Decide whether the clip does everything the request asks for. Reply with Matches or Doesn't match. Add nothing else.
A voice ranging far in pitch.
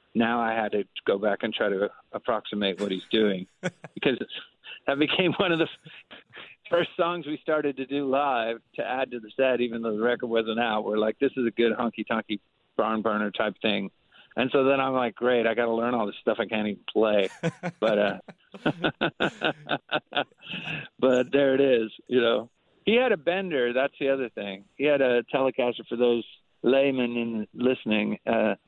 Doesn't match